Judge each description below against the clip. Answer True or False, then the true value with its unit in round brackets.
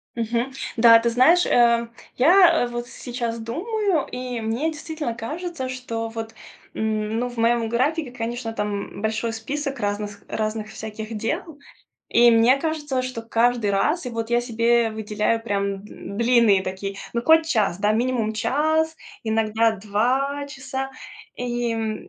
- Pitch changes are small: False (3.2 semitones)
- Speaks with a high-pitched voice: True (235 Hz)